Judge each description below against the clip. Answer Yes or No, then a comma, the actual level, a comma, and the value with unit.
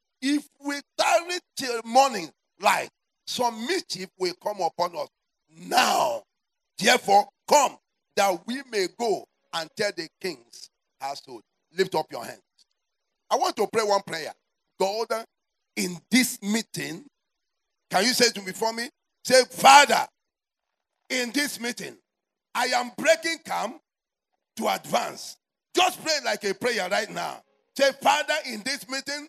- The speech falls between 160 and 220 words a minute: No, average, 140 wpm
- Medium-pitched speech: No, high, 245 Hz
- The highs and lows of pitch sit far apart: Yes, wide, 6.3 semitones